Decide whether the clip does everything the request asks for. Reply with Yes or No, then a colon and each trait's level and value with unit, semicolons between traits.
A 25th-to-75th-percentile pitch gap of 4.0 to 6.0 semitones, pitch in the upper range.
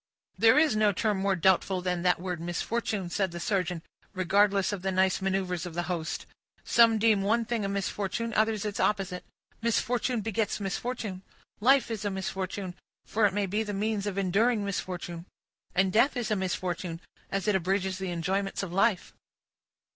No: average, 2.7 semitones; high, 195 Hz